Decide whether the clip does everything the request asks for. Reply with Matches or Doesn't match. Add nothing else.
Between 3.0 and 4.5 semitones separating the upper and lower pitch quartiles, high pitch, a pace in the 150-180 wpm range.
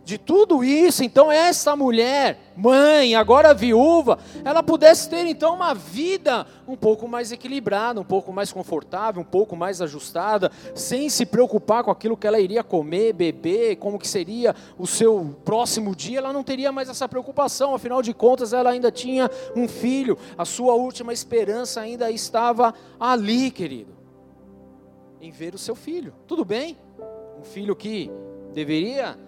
Doesn't match